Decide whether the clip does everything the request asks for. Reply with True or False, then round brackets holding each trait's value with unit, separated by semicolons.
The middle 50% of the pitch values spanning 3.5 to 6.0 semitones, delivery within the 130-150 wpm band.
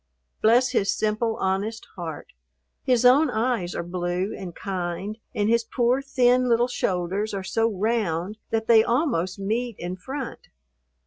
True (4.3 semitones; 145 wpm)